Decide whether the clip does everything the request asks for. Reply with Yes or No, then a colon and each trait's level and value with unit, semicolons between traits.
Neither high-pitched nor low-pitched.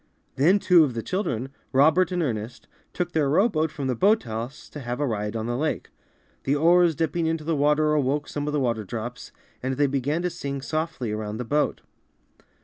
Yes: medium, 145 Hz